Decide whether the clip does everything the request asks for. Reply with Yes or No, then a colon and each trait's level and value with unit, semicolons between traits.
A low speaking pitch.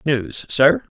Yes: low, 130 Hz